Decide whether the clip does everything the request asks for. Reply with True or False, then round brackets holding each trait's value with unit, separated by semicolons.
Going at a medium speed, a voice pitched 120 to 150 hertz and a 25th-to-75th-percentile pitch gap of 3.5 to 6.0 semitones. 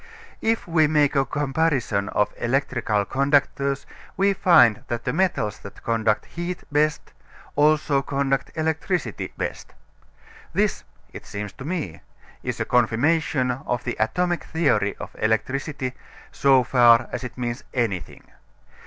False (130 wpm; 135 Hz; 4.8 semitones)